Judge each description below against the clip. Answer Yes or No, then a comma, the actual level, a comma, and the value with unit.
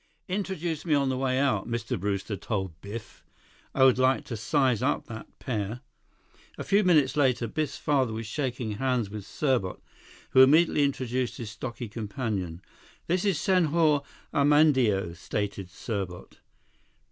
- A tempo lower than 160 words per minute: Yes, average, 145 wpm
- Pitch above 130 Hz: No, low, 125 Hz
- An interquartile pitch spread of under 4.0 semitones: No, wide, 5.4 semitones